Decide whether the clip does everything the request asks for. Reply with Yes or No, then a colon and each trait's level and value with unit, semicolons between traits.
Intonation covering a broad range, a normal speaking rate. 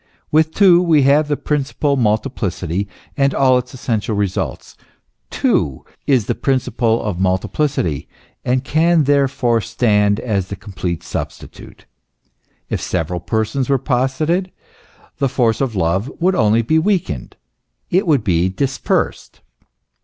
No: wide, 5.8 semitones; slow, 130 wpm